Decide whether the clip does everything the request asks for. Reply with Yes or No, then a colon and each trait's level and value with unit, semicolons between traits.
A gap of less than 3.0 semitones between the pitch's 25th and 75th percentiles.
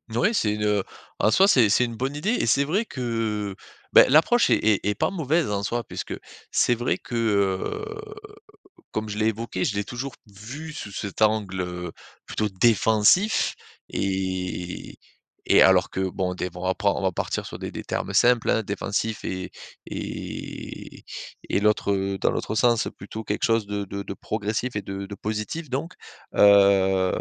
No: average, 3.7 semitones